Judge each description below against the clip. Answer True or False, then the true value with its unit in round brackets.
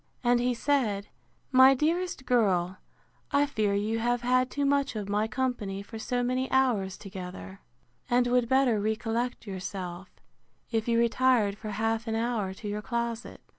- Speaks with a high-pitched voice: True (230 Hz)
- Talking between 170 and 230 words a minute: False (160 wpm)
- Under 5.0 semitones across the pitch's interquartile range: True (3.6 semitones)